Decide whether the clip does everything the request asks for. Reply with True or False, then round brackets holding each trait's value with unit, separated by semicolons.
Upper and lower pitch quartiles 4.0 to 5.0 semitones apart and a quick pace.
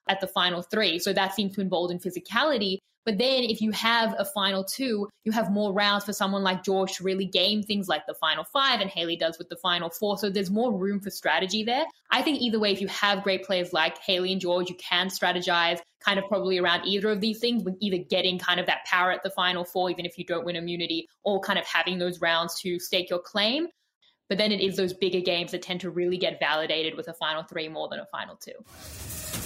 False (2.6 semitones; 250 wpm)